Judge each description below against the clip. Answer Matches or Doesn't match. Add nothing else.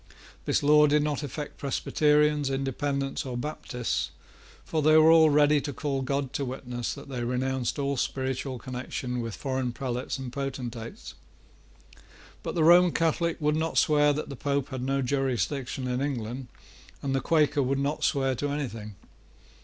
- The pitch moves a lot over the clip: Doesn't match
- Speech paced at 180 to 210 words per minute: Doesn't match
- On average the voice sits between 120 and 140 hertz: Matches